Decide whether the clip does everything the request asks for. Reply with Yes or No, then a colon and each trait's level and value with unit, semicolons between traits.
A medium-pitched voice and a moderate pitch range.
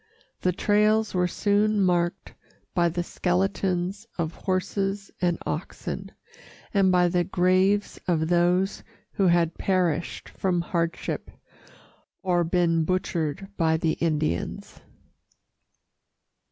No: medium, 180 Hz; narrow, 2.1 semitones